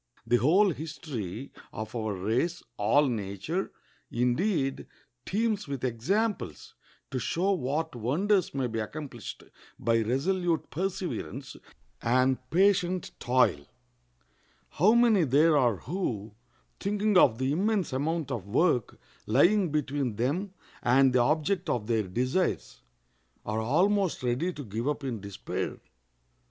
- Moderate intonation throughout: No, wide, 7.2 semitones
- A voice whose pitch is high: No, medium, 140 Hz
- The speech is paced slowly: Yes, slow, 120 wpm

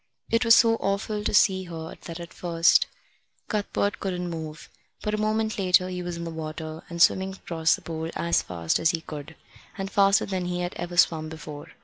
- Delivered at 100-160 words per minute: No, fast, 205 wpm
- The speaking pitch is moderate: Yes, medium, 175 Hz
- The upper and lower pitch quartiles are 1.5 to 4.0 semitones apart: Yes, average, 3.3 semitones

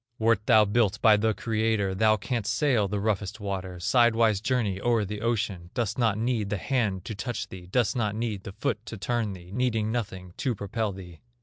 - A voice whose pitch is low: Yes, low, 110 Hz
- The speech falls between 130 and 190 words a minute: No, average, 200 wpm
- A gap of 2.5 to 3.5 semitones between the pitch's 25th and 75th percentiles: Yes, average, 2.8 semitones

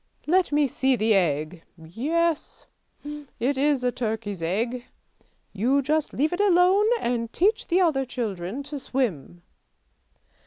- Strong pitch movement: Yes, wide, 6.2 semitones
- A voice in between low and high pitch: No, very high, 255 Hz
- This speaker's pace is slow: Yes, slow, 130 wpm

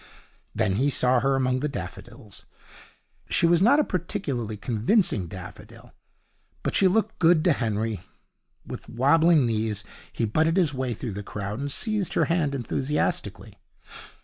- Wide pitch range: Yes, wide, 7.0 semitones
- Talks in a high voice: No, low, 135 Hz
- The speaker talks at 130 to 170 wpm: Yes, average, 150 wpm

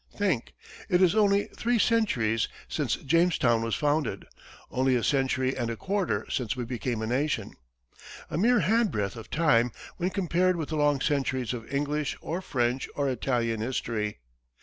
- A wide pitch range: Yes, wide, 6.5 semitones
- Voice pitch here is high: No, low, 135 Hz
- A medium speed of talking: Yes, average, 160 wpm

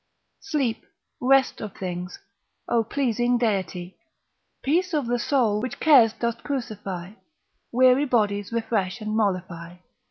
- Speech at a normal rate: No, slow, 120 wpm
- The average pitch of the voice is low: No, high, 230 Hz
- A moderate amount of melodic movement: Yes, average, 4.3 semitones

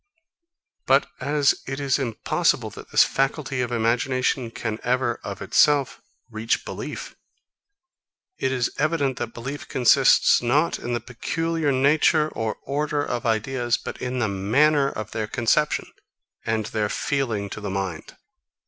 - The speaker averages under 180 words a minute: Yes, average, 145 wpm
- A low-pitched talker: Yes, low, 125 Hz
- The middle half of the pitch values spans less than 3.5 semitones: No, average, 4.0 semitones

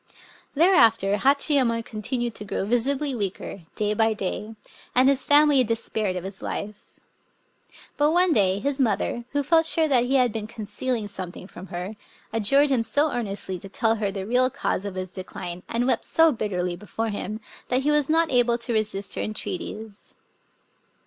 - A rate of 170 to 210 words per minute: Yes, average, 175 wpm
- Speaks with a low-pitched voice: No, high, 225 Hz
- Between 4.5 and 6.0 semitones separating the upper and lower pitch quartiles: Yes, average, 4.8 semitones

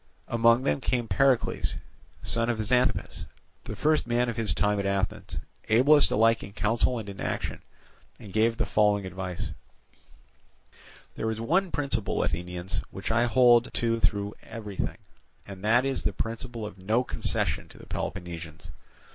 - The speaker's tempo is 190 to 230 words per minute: No, average, 155 wpm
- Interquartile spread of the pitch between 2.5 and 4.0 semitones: Yes, average, 3.2 semitones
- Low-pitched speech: Yes, low, 115 Hz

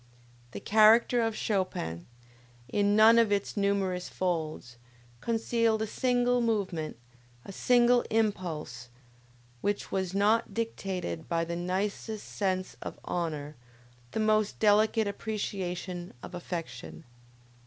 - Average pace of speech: No, slow, 110 wpm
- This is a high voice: Yes, high, 200 Hz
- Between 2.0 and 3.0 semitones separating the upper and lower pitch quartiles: No, average, 3.9 semitones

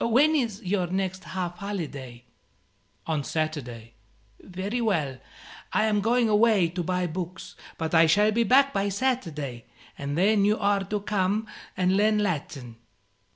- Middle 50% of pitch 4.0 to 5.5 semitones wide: Yes, average, 4.8 semitones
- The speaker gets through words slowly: No, average, 150 wpm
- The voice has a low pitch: No, high, 190 Hz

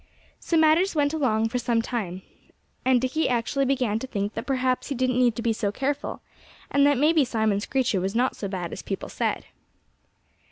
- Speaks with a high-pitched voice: Yes, very high, 250 Hz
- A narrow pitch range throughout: No, average, 4.0 semitones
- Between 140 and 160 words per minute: No, average, 195 wpm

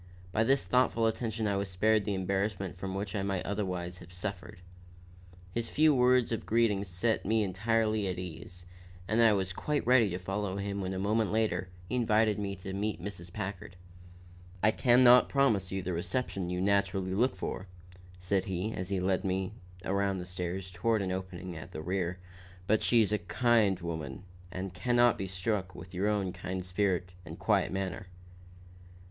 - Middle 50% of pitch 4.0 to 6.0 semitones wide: No, average, 3.1 semitones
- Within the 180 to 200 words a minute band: Yes, average, 190 wpm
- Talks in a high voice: No, very low, 95 Hz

